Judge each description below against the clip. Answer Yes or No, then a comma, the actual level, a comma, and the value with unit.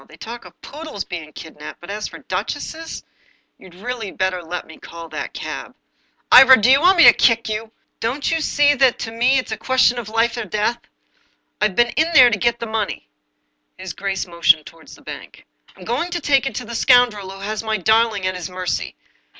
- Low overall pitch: No, high, 225 Hz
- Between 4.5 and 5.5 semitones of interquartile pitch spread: Yes, average, 5.2 semitones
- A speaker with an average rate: No, fast, 225 wpm